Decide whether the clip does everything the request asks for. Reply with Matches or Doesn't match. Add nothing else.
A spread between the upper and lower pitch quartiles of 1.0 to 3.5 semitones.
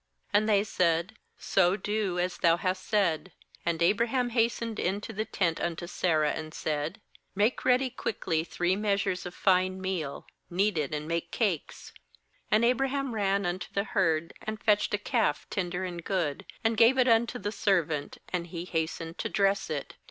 Doesn't match